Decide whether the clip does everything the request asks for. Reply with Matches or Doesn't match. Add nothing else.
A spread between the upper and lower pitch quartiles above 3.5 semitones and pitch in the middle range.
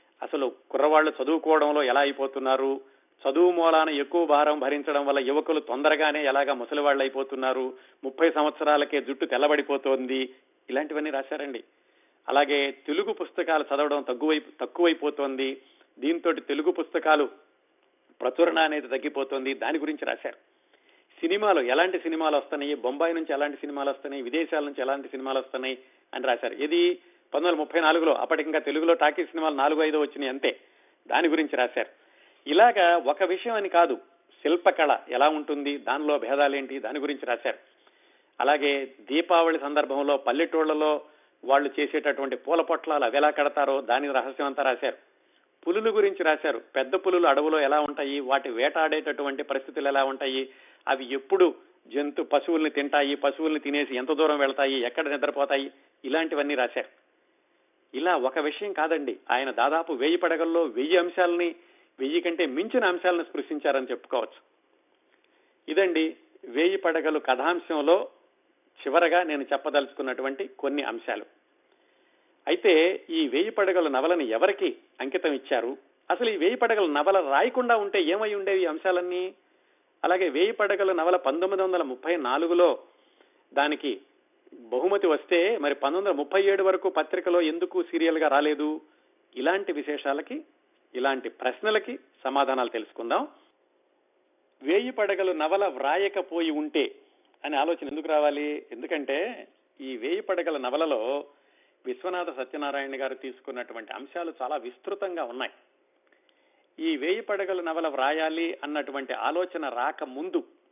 Matches